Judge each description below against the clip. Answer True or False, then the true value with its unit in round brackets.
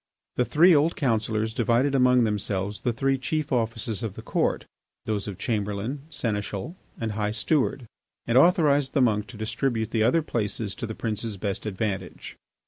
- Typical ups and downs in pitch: True (4.2 semitones)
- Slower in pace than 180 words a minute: True (165 wpm)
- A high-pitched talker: False (115 Hz)